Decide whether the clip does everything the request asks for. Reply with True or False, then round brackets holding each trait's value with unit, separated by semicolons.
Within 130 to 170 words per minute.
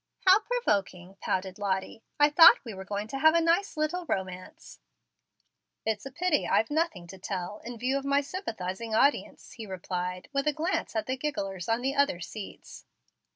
False (180 wpm)